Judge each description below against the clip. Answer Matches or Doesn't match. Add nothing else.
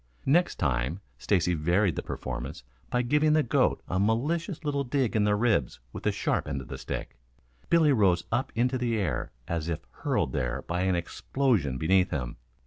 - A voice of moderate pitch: Doesn't match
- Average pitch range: Doesn't match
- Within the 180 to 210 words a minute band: Matches